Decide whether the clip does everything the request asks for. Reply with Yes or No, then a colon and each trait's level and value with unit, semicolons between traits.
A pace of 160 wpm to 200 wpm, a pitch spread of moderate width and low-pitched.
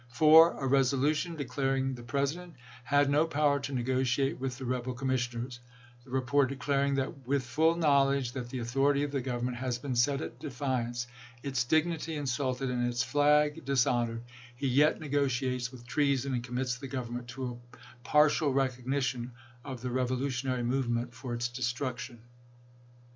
No: average, 165 wpm; narrow, 2.3 semitones; low, 130 Hz